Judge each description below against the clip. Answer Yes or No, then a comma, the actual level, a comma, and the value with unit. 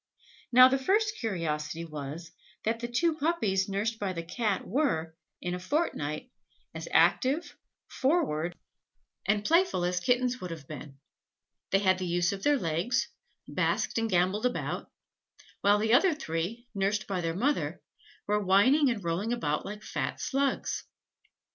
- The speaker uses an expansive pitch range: Yes, wide, 6.4 semitones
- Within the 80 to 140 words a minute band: No, average, 150 wpm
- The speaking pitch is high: Yes, high, 205 Hz